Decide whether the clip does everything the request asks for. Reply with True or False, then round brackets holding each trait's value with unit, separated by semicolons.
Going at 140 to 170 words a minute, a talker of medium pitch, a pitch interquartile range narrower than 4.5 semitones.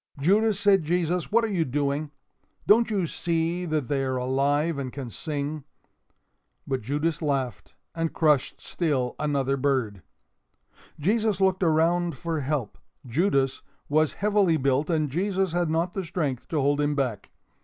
True (150 wpm; 155 Hz; 4.1 semitones)